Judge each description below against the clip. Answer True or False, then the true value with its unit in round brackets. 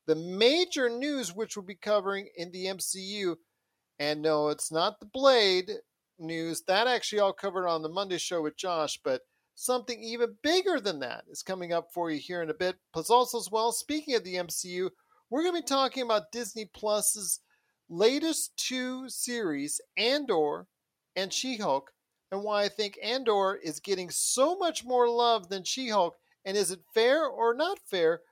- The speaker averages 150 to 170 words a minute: False (180 wpm)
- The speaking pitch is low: False (215 Hz)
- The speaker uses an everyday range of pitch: False (6.2 semitones)